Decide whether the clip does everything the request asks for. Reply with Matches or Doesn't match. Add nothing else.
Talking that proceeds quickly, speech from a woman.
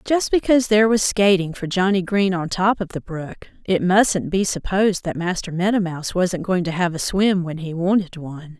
Matches